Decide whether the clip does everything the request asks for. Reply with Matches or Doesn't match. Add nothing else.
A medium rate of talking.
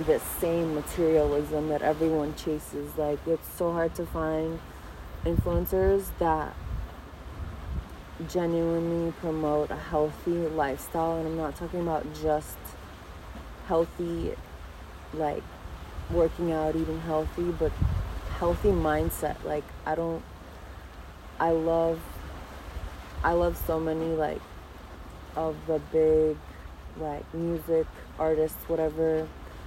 Doesn't match